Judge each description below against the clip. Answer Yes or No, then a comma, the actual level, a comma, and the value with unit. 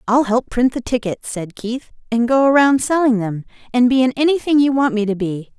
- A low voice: No, high, 240 Hz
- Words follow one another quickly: Yes, fast, 225 wpm